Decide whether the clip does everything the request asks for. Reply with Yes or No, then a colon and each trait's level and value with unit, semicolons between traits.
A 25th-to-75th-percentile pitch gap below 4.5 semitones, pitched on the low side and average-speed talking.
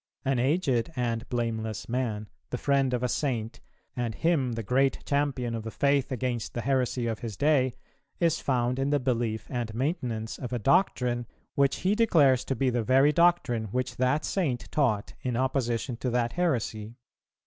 Yes: average, 2.9 semitones; low, 125 Hz; average, 175 wpm